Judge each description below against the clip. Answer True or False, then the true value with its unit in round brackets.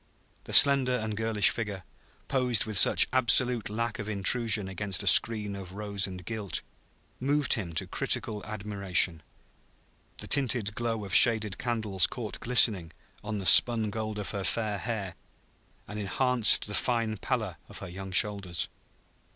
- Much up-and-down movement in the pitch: False (2.9 semitones)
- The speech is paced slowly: False (150 wpm)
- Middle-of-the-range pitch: False (105 Hz)